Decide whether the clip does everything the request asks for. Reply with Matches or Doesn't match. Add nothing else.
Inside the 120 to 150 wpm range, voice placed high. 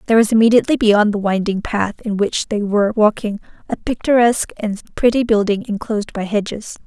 Doesn't match